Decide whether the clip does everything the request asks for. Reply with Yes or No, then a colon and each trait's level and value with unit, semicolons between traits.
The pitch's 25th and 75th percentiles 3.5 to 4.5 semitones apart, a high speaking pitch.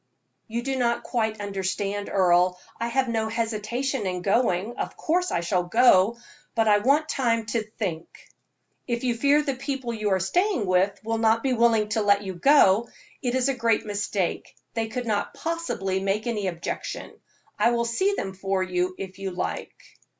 Yes: average, 3.8 semitones; high, 220 Hz